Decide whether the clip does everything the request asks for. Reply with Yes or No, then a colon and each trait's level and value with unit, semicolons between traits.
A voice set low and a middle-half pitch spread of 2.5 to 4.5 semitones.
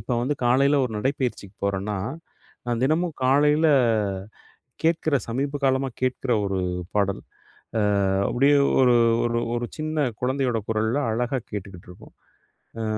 Yes: low, 125 Hz; average, 4.2 semitones